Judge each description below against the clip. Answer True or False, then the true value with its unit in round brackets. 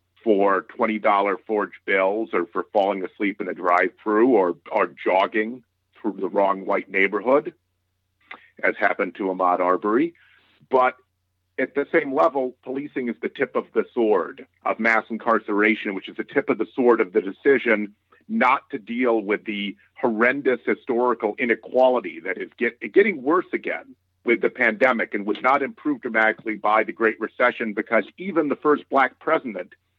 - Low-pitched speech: True (110 Hz)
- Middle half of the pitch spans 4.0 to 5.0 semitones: True (4.5 semitones)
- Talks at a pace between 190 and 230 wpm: False (160 wpm)